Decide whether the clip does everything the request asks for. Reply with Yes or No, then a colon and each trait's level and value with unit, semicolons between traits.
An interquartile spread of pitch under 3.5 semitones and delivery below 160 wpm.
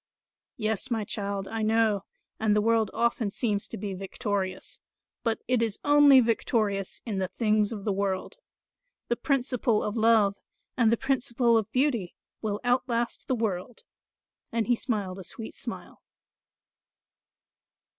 Yes: average, 2.8 semitones; average, 145 wpm